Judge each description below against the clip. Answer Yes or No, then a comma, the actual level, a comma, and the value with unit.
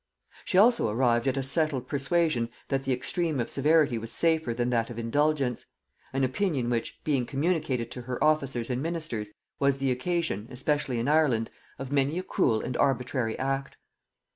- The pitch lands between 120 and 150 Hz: Yes, low, 135 Hz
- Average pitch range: Yes, average, 4.1 semitones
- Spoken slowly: No, average, 170 wpm